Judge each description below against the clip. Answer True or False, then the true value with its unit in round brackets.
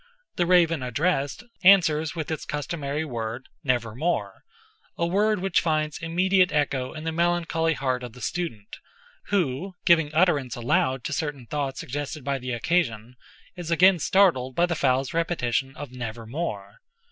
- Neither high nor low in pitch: True (150 Hz)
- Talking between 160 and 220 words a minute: False (145 wpm)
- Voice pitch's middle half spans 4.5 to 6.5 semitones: True (5.1 semitones)